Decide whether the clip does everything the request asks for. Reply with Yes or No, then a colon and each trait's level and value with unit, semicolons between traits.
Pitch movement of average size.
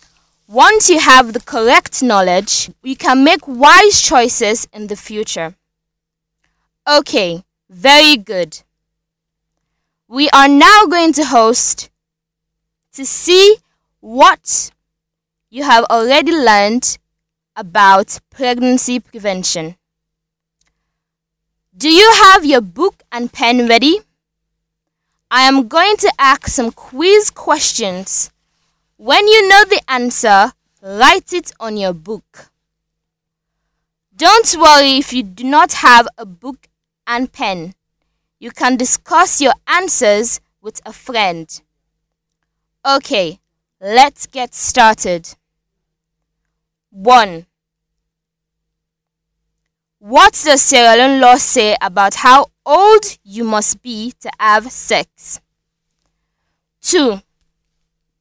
No: wide, 8.9 semitones